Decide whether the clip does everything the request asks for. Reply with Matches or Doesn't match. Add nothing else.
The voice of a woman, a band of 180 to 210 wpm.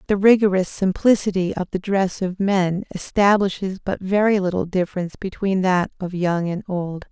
Doesn't match